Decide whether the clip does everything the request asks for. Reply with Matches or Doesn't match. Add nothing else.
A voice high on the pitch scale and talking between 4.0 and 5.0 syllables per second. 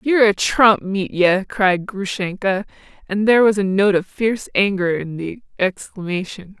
Matches